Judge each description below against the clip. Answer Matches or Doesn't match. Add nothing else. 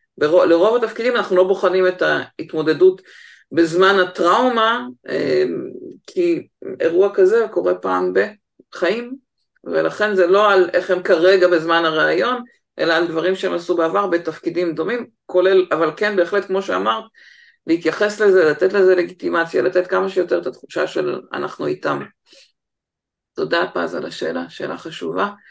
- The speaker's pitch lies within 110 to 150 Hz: Doesn't match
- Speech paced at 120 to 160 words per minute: Matches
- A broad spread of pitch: Doesn't match